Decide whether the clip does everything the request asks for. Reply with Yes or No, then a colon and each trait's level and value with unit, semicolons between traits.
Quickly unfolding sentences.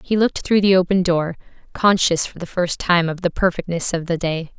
Yes: fast, 225 wpm